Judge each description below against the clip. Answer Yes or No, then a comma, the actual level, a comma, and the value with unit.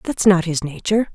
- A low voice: No, medium, 185 Hz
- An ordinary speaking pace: No, fast, 210 wpm